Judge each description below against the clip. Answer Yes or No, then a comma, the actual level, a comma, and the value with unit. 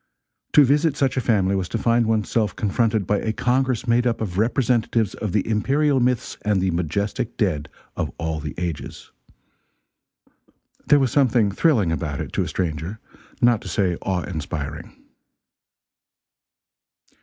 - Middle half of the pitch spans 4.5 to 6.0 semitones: Yes, average, 5.2 semitones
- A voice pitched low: Yes, low, 105 Hz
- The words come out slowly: No, average, 155 wpm